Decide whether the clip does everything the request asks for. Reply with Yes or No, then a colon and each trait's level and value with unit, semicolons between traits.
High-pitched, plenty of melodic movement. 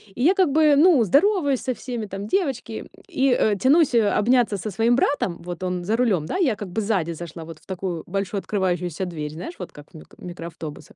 Yes: high, 205 Hz; wide, 6.8 semitones